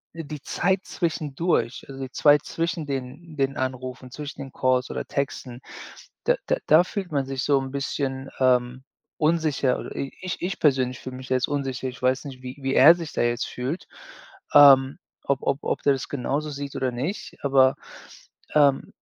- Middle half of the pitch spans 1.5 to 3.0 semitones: Yes, narrow, 2.6 semitones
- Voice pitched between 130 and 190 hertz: Yes, low, 135 Hz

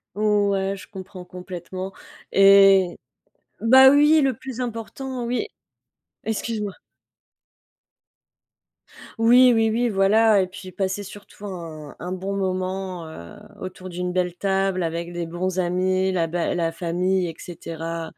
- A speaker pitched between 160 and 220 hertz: Yes, high, 190 Hz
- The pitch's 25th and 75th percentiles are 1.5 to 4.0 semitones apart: Yes, average, 2.9 semitones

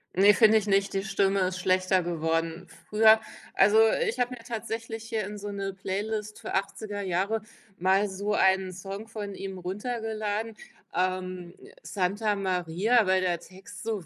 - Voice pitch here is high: Yes, high, 195 Hz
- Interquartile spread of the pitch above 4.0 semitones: No, average, 2.7 semitones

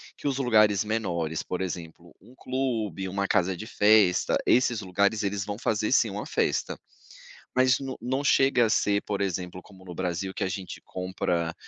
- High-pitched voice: No, low, 100 Hz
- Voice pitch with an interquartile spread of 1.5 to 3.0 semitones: No, average, 3.5 semitones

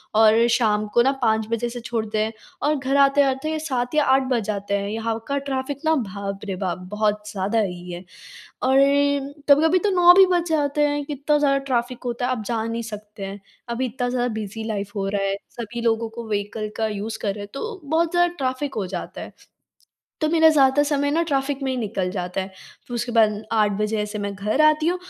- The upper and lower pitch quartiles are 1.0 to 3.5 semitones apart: No, average, 5.1 semitones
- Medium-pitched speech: No, high, 235 Hz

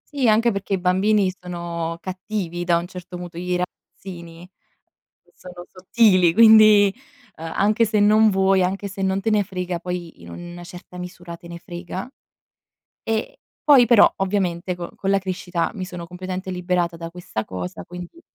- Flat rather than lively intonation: Yes, narrow, 2.3 semitones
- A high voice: No, medium, 180 Hz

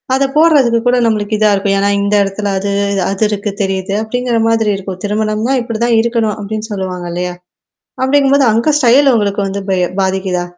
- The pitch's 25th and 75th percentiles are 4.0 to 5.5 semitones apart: No, average, 3.2 semitones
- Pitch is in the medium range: No, high, 215 Hz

